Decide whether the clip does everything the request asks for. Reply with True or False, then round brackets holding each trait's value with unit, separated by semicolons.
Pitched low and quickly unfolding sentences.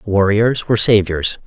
False (105 Hz; 125 wpm)